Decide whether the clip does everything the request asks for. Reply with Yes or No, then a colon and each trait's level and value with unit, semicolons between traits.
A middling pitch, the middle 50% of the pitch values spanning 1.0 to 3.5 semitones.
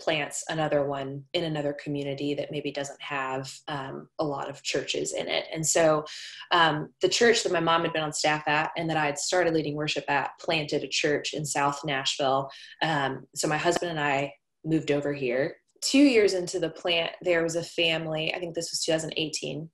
Yes: medium, 155 Hz; average, 2.7 semitones